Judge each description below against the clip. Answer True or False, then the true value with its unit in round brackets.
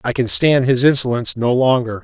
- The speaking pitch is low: True (125 Hz)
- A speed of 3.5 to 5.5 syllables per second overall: False (5.7 syllables/s)